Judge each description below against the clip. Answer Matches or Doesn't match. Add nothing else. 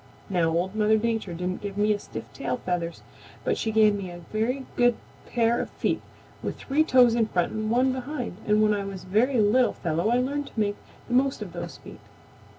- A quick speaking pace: Matches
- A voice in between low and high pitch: Doesn't match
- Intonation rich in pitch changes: Doesn't match